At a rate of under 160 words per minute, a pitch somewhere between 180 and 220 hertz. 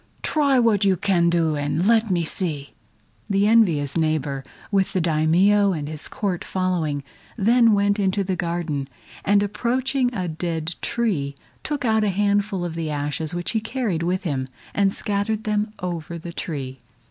No: average, 165 wpm; medium, 185 Hz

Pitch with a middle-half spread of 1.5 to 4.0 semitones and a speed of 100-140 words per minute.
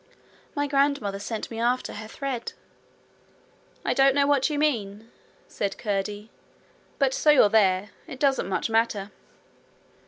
No: average, 5.1 semitones; slow, 135 wpm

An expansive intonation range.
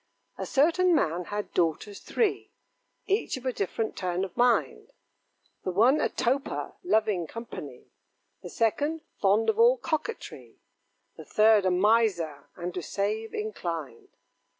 Yes: wide, 8.0 semitones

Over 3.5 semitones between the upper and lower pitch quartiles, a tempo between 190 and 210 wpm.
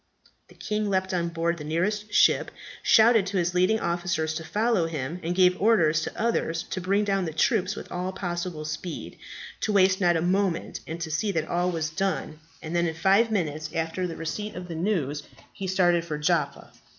No: average, 3.0 semitones; average, 200 wpm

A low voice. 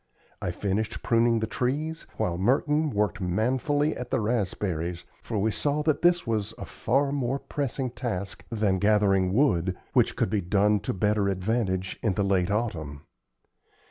Yes: low, 105 Hz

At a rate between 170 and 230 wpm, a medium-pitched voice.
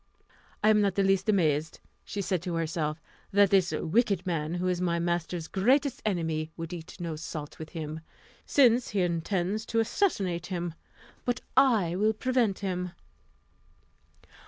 No: average, 160 wpm; medium, 180 Hz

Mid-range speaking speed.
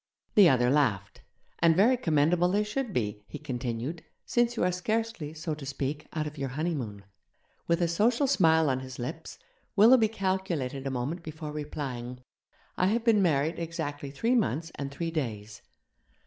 Yes: average, 165 wpm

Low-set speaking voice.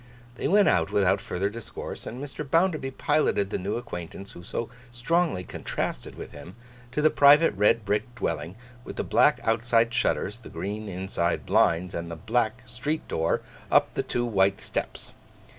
Yes: low, 110 Hz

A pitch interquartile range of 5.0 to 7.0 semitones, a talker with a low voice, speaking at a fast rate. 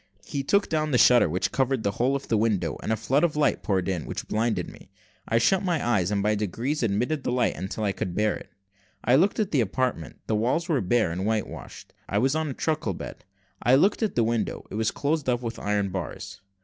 Yes: average, 5.3 semitones; low, 120 Hz; fast, 240 wpm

